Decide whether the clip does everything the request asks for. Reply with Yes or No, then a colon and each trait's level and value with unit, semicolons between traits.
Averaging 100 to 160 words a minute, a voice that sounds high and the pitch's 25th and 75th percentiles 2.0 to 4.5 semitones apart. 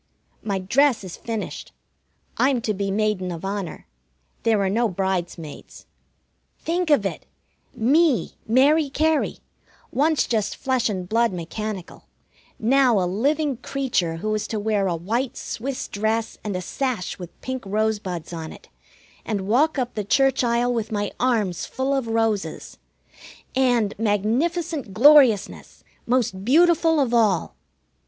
No: average, 140 wpm; high, 225 Hz; average, 5.0 semitones